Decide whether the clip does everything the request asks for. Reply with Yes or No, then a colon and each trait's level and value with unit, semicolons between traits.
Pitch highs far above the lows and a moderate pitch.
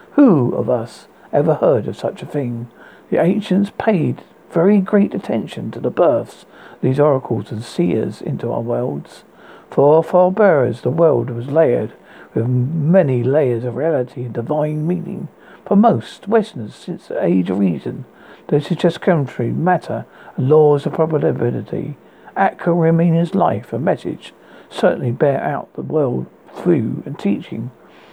Yes: wide, 6.4 semitones; medium, 155 Hz